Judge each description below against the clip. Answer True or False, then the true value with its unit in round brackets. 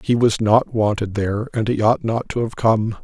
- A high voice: False (110 Hz)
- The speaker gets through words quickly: True (235 wpm)